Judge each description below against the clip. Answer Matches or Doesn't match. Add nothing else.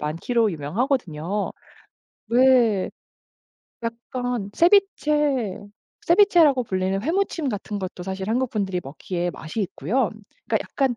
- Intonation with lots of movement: Matches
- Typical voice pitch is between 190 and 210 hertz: Doesn't match